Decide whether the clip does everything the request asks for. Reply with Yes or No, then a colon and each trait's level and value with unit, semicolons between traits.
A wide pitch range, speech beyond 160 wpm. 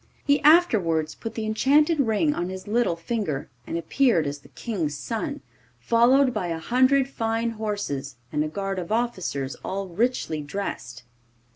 No: wide, 6.7 semitones; average, 155 wpm